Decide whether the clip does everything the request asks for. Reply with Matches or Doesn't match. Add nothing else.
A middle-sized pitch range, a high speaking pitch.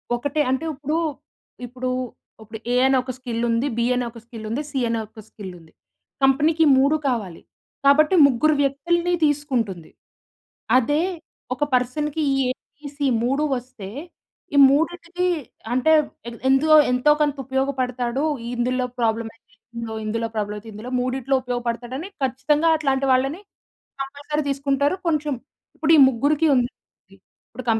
Matches